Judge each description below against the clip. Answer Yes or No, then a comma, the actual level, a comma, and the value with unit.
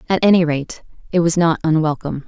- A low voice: No, medium, 165 Hz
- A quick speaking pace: No, average, 185 wpm